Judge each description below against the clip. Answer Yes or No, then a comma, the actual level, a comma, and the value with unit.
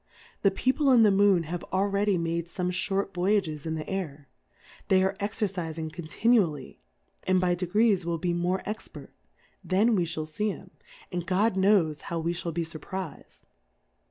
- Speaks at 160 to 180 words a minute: Yes, average, 165 wpm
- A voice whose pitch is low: No, medium, 185 Hz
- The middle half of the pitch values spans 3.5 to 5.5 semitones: No, average, 3.1 semitones